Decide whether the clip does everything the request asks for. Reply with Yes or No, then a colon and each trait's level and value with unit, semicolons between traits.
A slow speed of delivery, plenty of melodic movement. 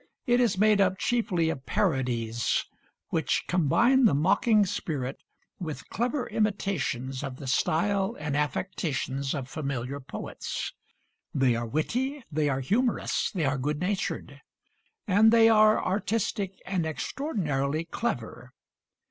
Yes: slow, 125 wpm; wide, 7.7 semitones